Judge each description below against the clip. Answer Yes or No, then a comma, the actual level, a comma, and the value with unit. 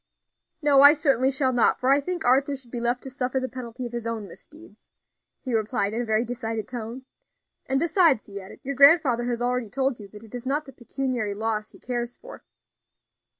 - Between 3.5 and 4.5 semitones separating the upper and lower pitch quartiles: No, average, 3.0 semitones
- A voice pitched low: No, very high, 250 Hz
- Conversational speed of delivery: No, fast, 210 wpm